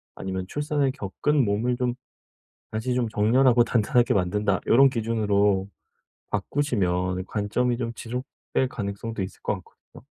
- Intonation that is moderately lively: Yes, average, 3.8 semitones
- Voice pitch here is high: No, low, 115 Hz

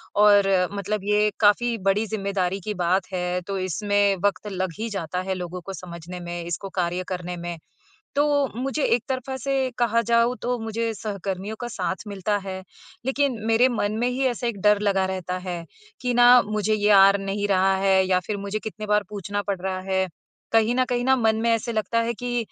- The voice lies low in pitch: No, high, 205 Hz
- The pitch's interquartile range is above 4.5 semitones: No, average, 3.5 semitones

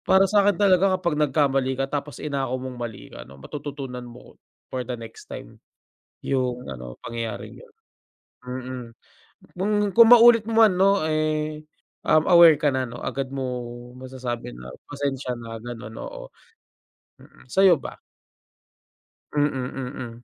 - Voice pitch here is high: No, low, 135 Hz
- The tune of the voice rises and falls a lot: No, average, 4.2 semitones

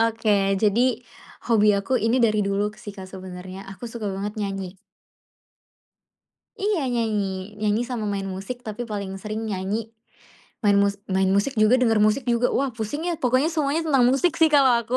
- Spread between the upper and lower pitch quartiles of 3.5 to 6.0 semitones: Yes, average, 3.8 semitones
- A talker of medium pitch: No, high, 215 Hz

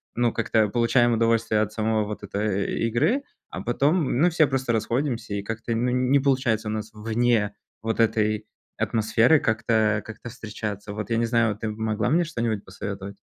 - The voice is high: No, low, 115 Hz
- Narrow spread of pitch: Yes, narrow, 2.1 semitones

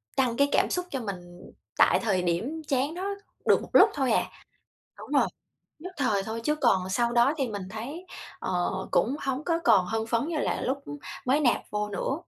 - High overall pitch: Yes, high, 240 Hz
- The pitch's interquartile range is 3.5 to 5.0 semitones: No, wide, 5.6 semitones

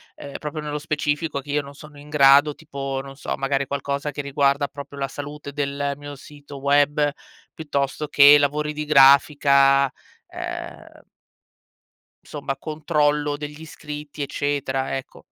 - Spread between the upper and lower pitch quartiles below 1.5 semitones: Yes, narrow, 1.1 semitones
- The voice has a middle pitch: Yes, medium, 145 Hz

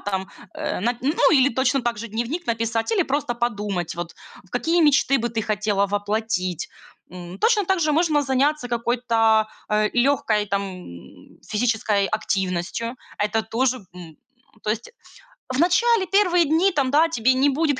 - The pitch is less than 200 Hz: No, high, 235 Hz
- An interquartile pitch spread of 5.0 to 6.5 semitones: Yes, wide, 5.5 semitones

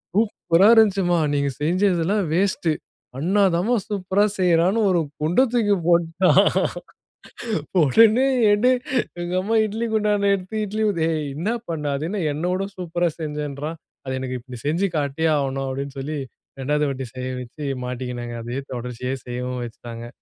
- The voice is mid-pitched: Yes, medium, 165 Hz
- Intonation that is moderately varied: No, wide, 6.5 semitones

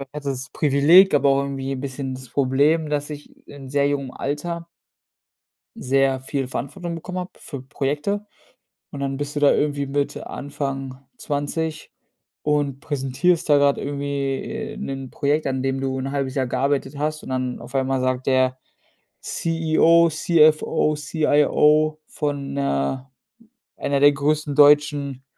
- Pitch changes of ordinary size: No, narrow, 2.0 semitones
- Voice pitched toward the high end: No, medium, 140 Hz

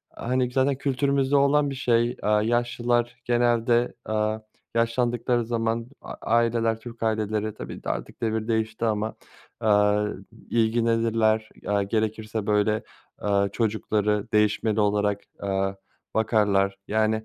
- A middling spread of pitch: No, narrow, 2.0 semitones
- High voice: No, low, 110 Hz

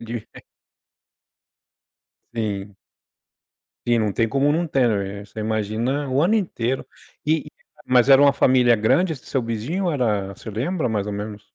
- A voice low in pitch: Yes, low, 120 Hz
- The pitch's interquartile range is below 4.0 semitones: No, average, 4.9 semitones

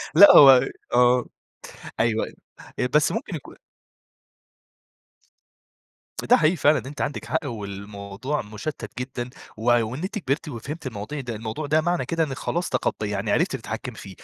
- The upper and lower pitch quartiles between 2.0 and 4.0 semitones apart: No, wide, 5.6 semitones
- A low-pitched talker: Yes, low, 130 Hz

